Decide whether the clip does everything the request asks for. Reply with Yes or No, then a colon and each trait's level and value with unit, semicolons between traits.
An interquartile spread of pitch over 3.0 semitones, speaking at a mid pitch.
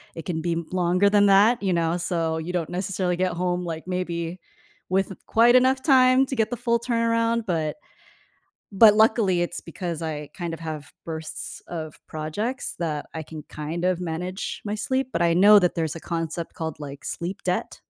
Yes: average, 4.2 semitones; medium, 180 Hz